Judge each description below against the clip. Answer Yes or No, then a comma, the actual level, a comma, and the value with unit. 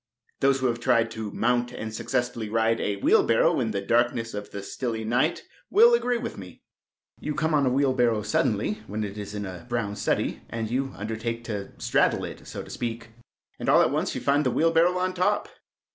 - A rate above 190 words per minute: Yes, fast, 205 wpm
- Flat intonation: No, average, 3.9 semitones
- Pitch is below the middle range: Yes, low, 115 Hz